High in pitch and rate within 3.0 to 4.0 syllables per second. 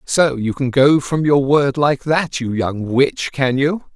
No: medium, 140 Hz; 3.7 syllables/s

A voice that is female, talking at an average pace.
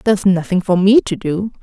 No: female; fast, 220 wpm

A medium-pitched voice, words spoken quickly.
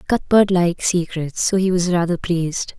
No: medium, 175 Hz; average, 170 wpm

